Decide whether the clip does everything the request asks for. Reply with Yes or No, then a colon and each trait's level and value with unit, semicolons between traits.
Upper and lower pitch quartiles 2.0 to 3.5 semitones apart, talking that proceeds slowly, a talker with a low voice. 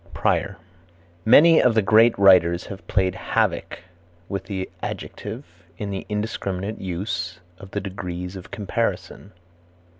Yes: narrow, 2.6 semitones; slow, 125 wpm; low, 100 Hz